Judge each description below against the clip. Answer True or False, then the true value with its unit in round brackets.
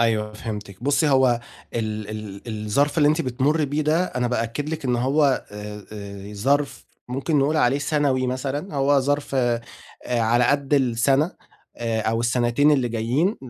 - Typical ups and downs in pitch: True (4.1 semitones)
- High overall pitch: False (130 Hz)